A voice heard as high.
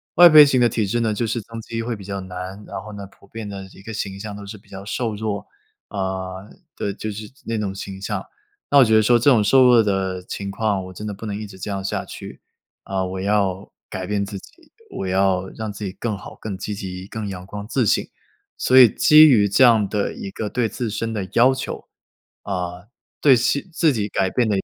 No: low, 105 Hz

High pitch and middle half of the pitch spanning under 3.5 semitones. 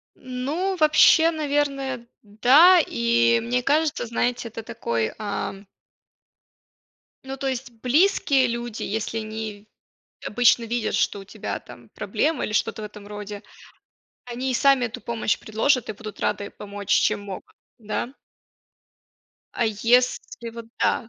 No: high, 235 Hz; average, 4.1 semitones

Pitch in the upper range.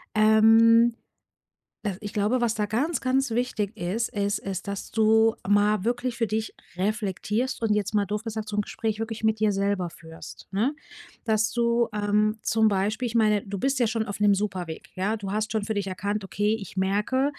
Yes: high, 215 Hz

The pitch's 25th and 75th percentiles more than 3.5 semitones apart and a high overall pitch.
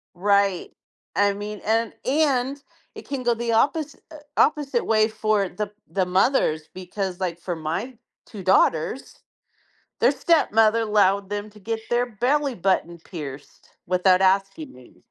Yes: average, 4.3 semitones; high, 210 Hz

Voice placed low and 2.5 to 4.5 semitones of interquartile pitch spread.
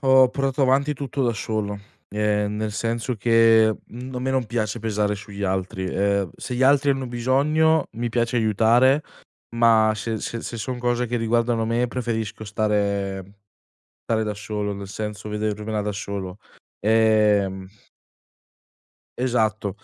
Yes: low, 110 Hz; average, 2.9 semitones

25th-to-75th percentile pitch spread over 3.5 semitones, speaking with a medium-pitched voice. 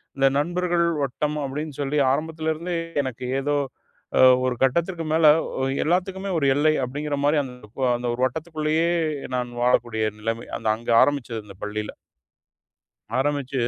Yes: average, 4.1 semitones; medium, 145 Hz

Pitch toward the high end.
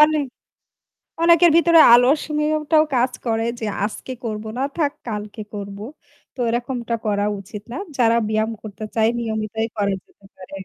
Yes: high, 230 Hz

